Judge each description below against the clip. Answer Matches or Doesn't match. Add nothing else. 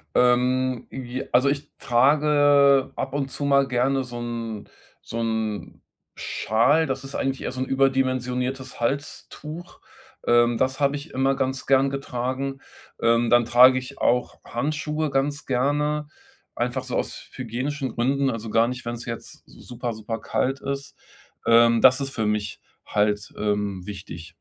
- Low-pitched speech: Matches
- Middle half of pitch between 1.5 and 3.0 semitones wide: Matches